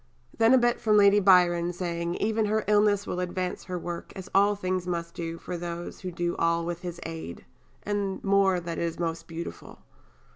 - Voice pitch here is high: No, medium, 180 Hz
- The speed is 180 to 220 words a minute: Yes, average, 185 wpm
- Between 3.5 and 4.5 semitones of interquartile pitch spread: No, average, 2.9 semitones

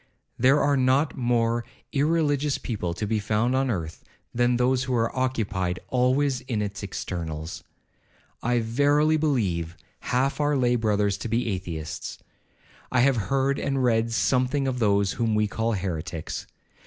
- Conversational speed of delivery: Yes, average, 150 wpm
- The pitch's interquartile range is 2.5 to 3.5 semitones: No, average, 4.5 semitones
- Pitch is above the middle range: No, low, 120 Hz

